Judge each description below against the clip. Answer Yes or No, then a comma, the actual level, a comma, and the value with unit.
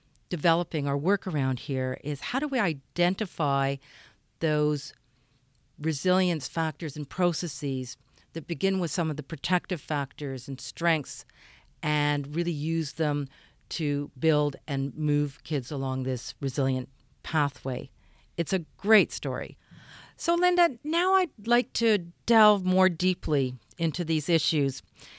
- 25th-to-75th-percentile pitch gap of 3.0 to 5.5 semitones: Yes, average, 4.1 semitones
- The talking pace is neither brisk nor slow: No, slow, 130 wpm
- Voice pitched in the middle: Yes, medium, 155 Hz